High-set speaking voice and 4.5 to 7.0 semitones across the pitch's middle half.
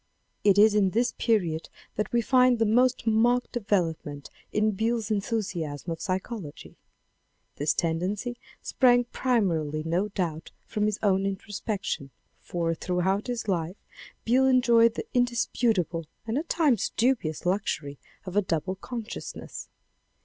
Yes: high, 205 Hz; average, 5.2 semitones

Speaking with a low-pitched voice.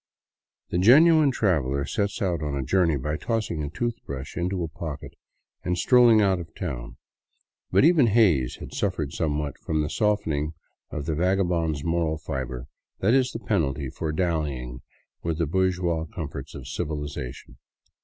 Yes: very low, 80 Hz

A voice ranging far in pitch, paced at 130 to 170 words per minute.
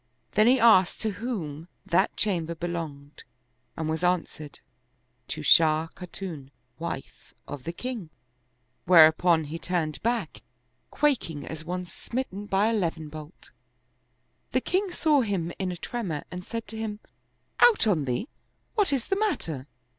Yes: wide, 5.9 semitones; average, 145 wpm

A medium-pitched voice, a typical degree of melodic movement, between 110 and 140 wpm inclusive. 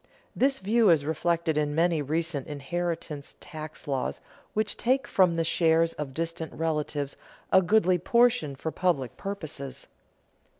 Yes: medium, 165 Hz; average, 3.5 semitones; slow, 135 wpm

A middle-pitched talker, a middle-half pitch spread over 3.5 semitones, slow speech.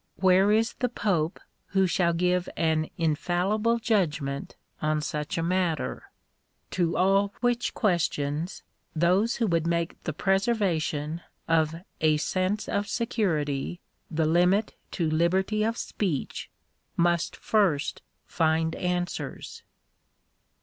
Yes: medium, 175 Hz; average, 4.0 semitones; slow, 115 wpm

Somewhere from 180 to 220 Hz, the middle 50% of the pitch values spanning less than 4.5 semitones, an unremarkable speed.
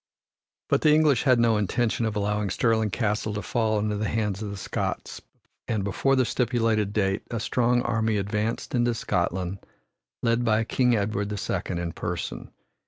No: low, 110 Hz; narrow, 2.4 semitones; average, 170 wpm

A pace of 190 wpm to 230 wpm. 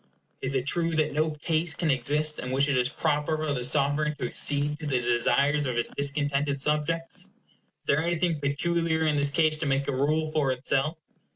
Yes: average, 200 wpm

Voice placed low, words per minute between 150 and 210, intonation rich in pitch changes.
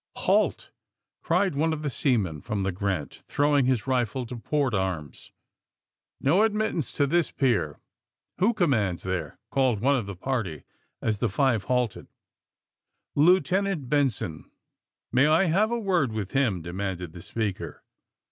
Yes: low, 125 Hz; average, 155 wpm; wide, 7.4 semitones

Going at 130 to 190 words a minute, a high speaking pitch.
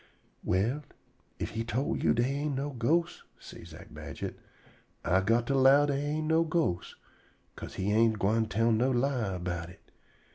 No: average, 170 wpm; low, 120 Hz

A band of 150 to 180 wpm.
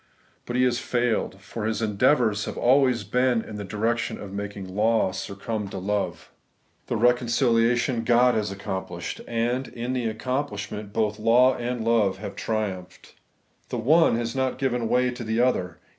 Yes: average, 160 wpm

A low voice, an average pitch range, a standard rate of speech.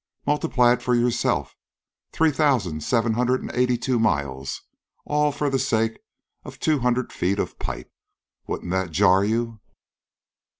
Yes: low, 120 Hz; average, 4.6 semitones; average, 145 wpm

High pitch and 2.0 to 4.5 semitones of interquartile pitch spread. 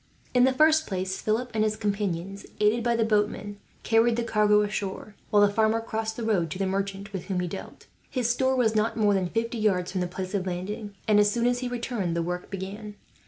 Yes: high, 210 Hz; average, 2.7 semitones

